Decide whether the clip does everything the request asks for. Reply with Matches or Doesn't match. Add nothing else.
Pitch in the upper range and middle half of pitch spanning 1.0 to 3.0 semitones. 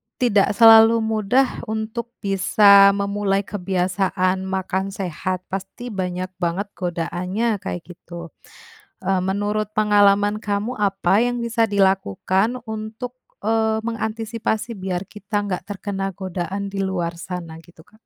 Matches